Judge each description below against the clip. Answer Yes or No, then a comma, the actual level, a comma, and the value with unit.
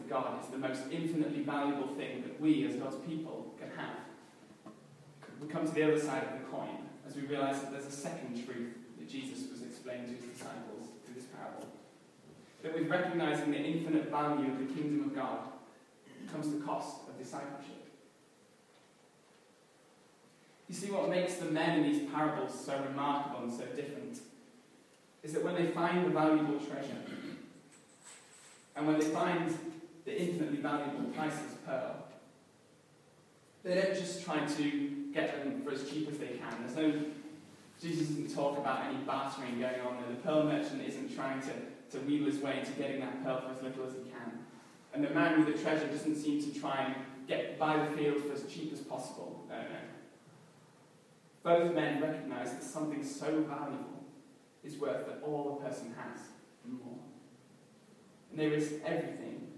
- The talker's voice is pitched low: No, medium, 150 Hz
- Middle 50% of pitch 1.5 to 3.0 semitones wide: Yes, average, 2.7 semitones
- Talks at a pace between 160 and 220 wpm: Yes, average, 175 wpm